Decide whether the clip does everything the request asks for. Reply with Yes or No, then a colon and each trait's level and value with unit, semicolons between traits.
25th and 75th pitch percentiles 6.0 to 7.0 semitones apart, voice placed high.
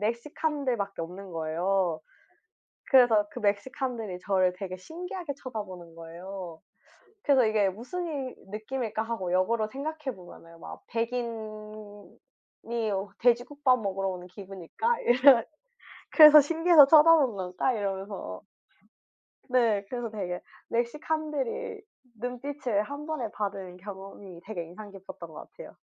No: wide, 5.4 semitones; high, 220 Hz